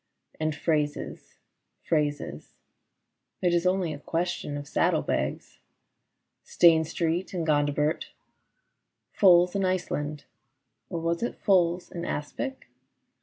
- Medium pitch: Yes, medium, 165 Hz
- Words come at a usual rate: No, slow, 115 wpm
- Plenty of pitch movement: No, average, 3.2 semitones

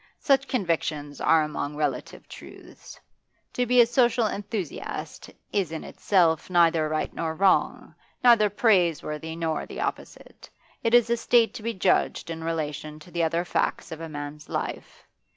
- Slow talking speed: No, average, 155 wpm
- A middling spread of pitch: No, wide, 6.1 semitones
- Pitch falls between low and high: Yes, medium, 170 Hz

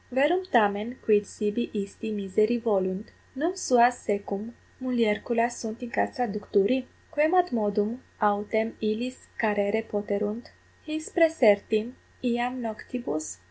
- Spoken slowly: Yes, slow, 105 wpm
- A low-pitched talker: No, high, 220 Hz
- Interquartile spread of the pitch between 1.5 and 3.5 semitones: Yes, average, 3.2 semitones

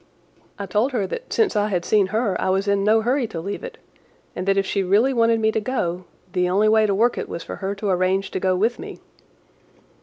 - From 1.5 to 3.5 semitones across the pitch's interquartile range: Yes, average, 2.9 semitones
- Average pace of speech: No, fast, 245 wpm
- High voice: Yes, high, 205 Hz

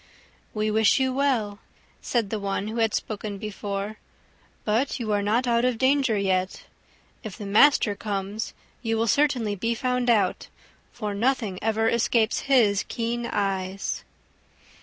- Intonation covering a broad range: No, average, 2.8 semitones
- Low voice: No, high, 220 Hz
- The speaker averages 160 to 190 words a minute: No, average, 145 wpm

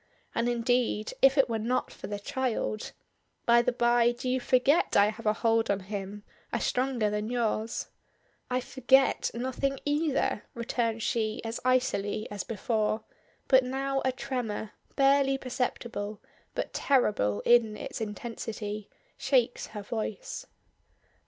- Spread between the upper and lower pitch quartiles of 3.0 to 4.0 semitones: Yes, average, 3.3 semitones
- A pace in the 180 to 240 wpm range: No, average, 140 wpm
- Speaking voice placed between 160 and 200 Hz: No, high, 235 Hz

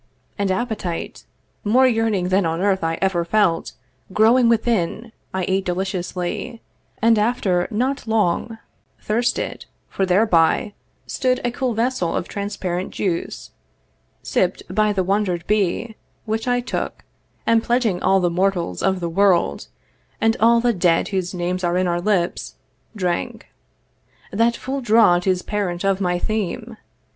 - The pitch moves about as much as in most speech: Yes, average, 4.0 semitones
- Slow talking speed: No, average, 145 wpm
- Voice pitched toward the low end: No, high, 200 Hz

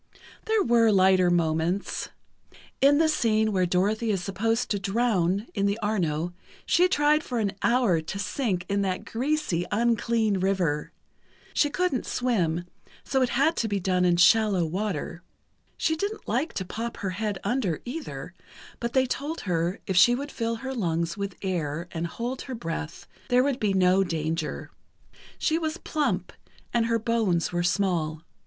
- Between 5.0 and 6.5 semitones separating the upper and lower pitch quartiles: Yes, wide, 5.5 semitones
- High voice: Yes, high, 205 Hz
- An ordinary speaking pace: Yes, average, 165 wpm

